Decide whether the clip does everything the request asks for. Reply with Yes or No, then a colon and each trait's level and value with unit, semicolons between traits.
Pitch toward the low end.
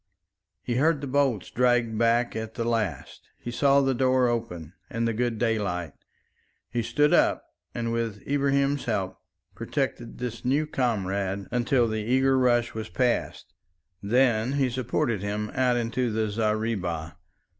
Yes: low, 115 Hz